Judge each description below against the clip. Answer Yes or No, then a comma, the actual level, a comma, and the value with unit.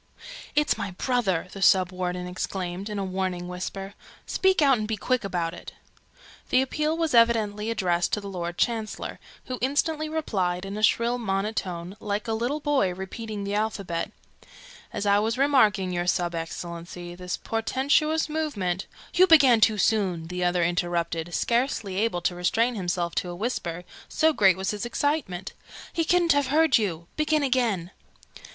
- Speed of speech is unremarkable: Yes, average, 165 wpm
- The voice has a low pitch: No, high, 205 Hz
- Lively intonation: Yes, wide, 5.9 semitones